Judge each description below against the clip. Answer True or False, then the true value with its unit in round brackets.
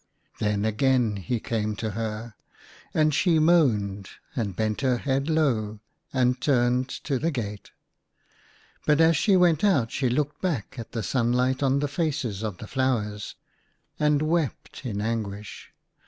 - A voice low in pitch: True (125 Hz)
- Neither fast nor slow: True (150 wpm)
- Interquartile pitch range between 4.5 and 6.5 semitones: True (5.3 semitones)